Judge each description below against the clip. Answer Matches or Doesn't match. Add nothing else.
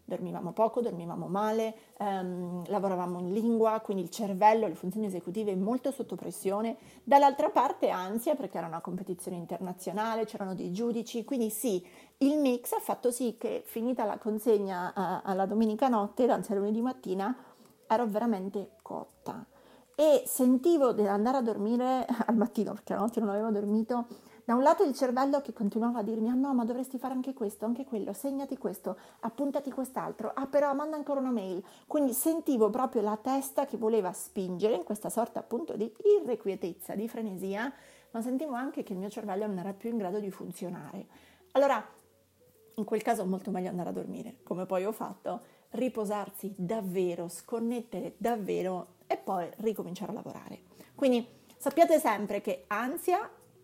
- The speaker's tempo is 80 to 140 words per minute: Doesn't match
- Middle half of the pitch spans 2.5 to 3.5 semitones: Doesn't match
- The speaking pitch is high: Matches